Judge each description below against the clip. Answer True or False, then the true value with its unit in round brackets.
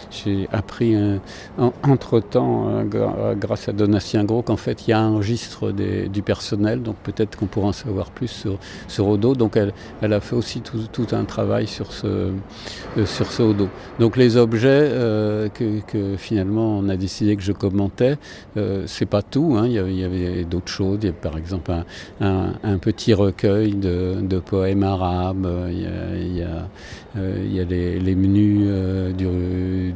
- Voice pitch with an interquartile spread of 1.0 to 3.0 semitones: True (2.6 semitones)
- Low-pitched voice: True (100 Hz)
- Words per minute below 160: False (205 wpm)